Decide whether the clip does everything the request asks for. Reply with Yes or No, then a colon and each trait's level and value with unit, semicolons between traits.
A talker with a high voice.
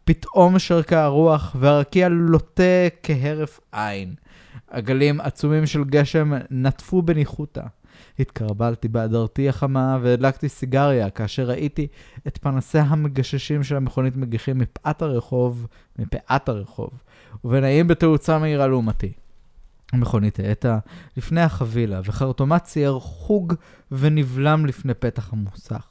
No: low, 135 Hz